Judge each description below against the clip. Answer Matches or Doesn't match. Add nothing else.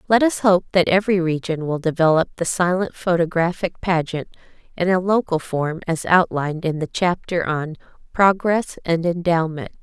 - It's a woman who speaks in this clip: Matches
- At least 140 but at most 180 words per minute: Matches